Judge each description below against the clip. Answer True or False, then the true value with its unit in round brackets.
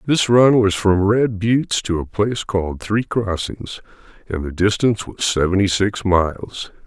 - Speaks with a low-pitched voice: True (100 Hz)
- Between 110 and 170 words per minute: True (165 wpm)